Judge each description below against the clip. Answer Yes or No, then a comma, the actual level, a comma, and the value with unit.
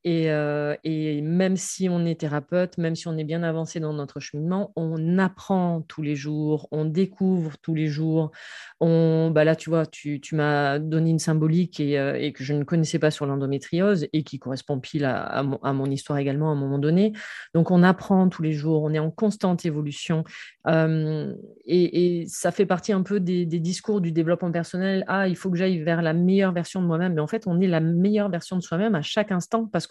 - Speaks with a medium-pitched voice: Yes, medium, 165 Hz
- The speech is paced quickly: Yes, fast, 225 wpm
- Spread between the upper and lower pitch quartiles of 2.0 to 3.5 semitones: Yes, average, 3.1 semitones